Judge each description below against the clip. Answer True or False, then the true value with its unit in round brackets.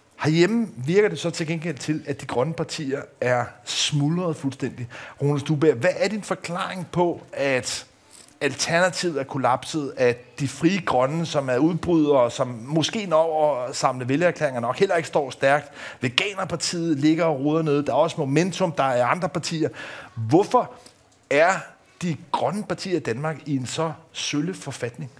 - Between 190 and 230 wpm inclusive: False (160 wpm)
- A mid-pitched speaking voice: True (150 Hz)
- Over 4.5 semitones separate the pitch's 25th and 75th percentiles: False (3.7 semitones)